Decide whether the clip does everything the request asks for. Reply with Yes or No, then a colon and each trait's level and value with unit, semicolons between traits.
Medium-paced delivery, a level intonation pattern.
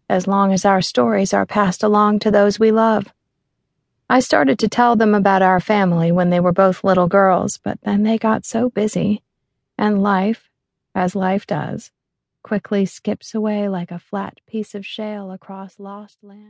Yes: average, 180 wpm; narrow, 2.1 semitones